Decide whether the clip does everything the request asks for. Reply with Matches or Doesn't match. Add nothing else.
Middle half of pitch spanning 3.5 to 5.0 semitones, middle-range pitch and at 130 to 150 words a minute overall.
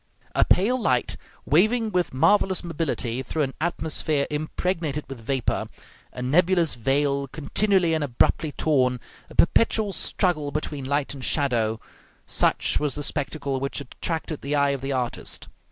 Matches